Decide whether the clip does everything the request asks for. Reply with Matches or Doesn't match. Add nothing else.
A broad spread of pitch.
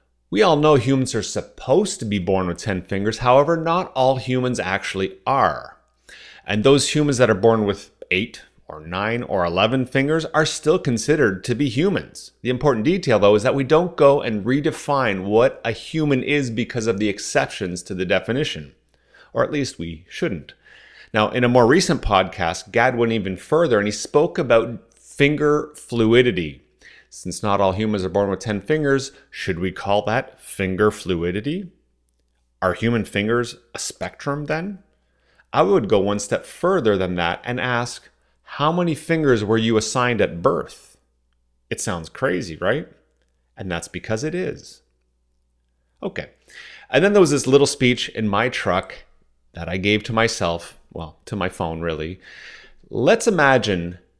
Matches